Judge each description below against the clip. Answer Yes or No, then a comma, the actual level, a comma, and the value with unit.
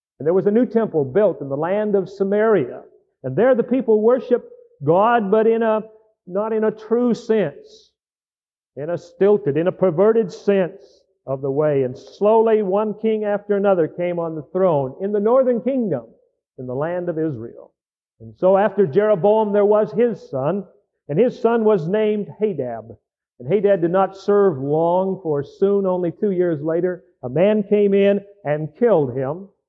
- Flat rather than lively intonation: No, average, 4.1 semitones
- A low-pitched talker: No, high, 200 Hz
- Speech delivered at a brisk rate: No, average, 180 wpm